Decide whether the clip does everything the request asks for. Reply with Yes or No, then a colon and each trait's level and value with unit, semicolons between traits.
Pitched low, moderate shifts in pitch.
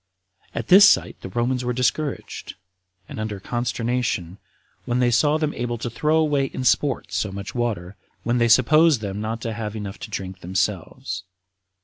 Yes: low, 120 Hz; average, 3.9 semitones